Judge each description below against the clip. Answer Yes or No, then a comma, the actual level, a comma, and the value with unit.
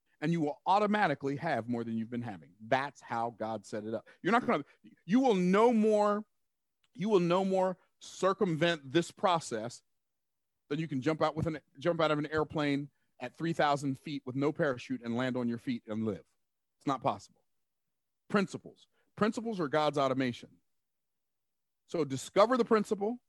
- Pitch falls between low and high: Yes, medium, 150 Hz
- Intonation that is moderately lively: No, wide, 6.5 semitones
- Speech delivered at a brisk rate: No, average, 180 wpm